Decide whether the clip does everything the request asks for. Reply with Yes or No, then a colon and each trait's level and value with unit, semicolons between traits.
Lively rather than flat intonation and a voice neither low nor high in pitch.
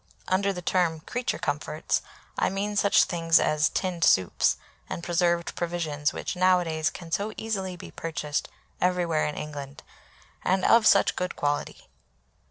No: average, 3.3 semitones; medium, 175 Hz